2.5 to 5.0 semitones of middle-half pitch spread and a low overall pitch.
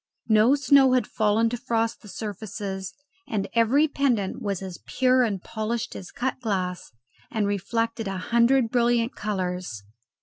No: average, 3.5 semitones; high, 225 Hz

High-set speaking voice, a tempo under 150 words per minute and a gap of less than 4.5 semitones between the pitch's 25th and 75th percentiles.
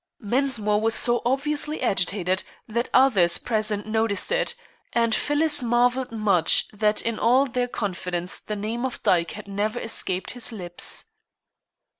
Yes: high, 225 Hz; average, 140 wpm; average, 3.6 semitones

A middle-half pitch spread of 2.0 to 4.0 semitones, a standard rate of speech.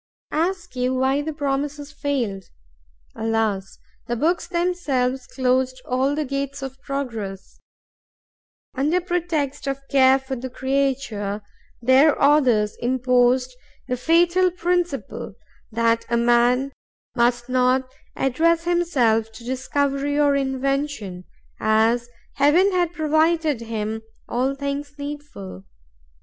No: average, 3.4 semitones; slow, 110 wpm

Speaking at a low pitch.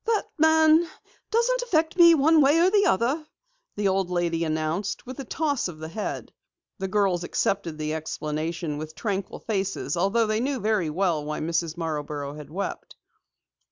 No: high, 195 Hz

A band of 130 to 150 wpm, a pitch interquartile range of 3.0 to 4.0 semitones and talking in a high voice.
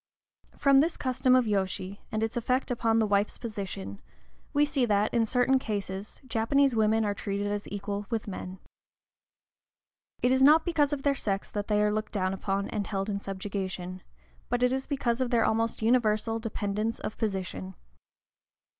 No: average, 170 wpm; average, 3.7 semitones; high, 215 Hz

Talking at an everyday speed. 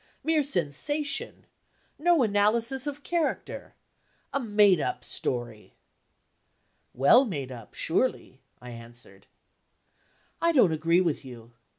No: slow, 105 wpm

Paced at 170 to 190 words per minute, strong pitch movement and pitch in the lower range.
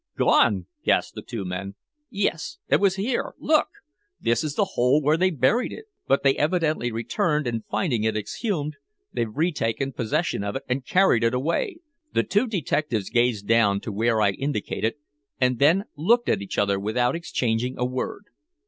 Yes: average, 175 wpm; wide, 6.6 semitones; low, 130 Hz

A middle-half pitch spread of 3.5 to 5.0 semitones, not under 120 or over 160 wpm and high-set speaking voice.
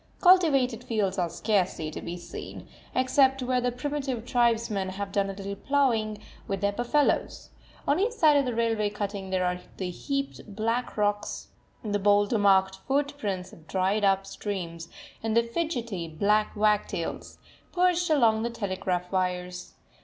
Yes: average, 4.6 semitones; average, 155 wpm; high, 210 Hz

